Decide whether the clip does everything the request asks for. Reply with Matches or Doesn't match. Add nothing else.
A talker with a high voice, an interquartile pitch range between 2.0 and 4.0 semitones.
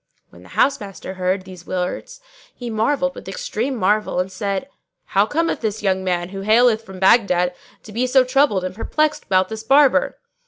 Doesn't match